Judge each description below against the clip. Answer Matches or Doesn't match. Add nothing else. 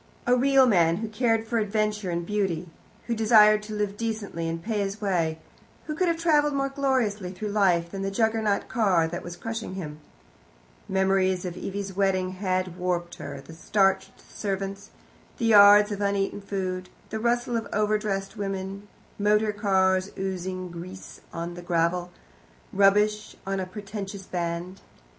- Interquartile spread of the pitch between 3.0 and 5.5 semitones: Doesn't match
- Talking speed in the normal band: Matches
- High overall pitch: Matches